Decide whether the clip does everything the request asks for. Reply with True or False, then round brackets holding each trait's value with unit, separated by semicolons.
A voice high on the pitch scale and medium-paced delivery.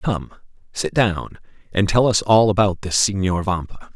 False (100 Hz; 165 wpm)